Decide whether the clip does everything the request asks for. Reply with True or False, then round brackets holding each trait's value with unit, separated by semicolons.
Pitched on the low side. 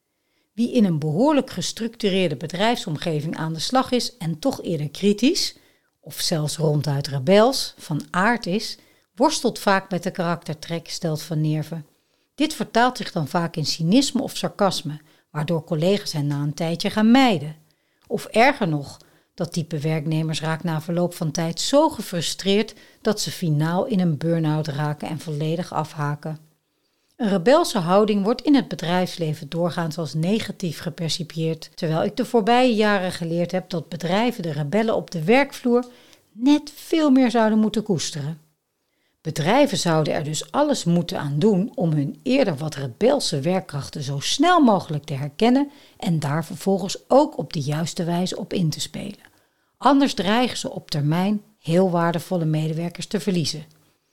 False (175 Hz)